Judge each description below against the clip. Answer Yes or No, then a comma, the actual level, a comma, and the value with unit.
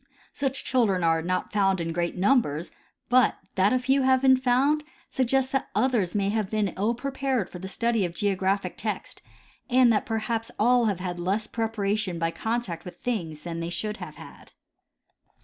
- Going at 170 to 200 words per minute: Yes, average, 180 wpm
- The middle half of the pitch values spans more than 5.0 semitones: Yes, wide, 5.4 semitones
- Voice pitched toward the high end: Yes, high, 215 Hz